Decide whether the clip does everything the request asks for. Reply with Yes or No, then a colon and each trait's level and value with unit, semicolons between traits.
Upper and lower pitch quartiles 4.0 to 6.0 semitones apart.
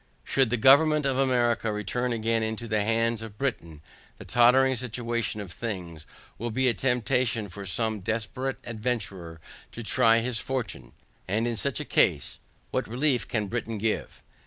No: narrow, 2.6 semitones